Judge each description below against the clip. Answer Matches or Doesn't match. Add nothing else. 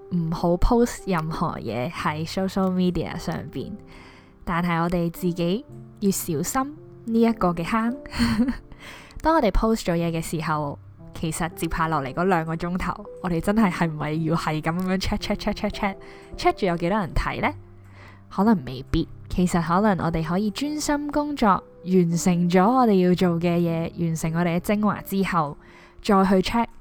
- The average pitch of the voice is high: Doesn't match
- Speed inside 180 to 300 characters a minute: Doesn't match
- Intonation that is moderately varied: Matches